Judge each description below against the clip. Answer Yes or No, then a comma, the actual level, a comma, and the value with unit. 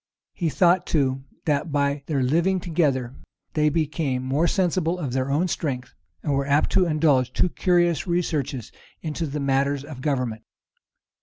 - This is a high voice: No, medium, 150 Hz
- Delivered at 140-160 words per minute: Yes, average, 150 wpm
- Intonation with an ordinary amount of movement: Yes, average, 3.9 semitones